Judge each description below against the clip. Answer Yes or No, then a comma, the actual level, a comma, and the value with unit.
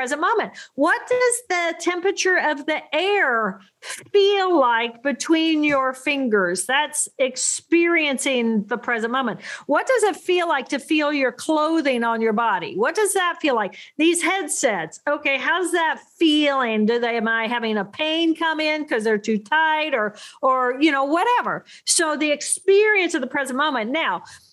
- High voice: Yes, very high, 300 Hz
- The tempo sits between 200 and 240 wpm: No, average, 165 wpm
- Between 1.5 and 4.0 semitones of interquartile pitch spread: No, average, 5.0 semitones